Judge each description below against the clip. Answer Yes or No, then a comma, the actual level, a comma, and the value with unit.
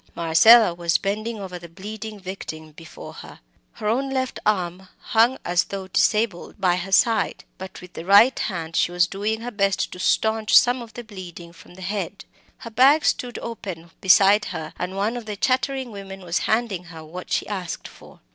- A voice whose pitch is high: Yes, high, 195 Hz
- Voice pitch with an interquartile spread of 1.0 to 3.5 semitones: No, average, 4.0 semitones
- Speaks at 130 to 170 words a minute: No, average, 190 wpm